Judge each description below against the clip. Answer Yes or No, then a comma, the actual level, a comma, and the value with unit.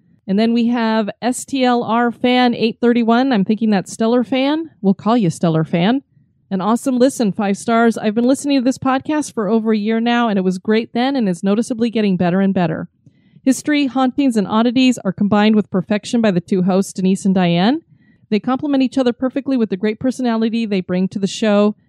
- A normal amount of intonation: Yes, average, 4.1 semitones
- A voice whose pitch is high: Yes, high, 225 Hz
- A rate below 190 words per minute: No, fast, 205 wpm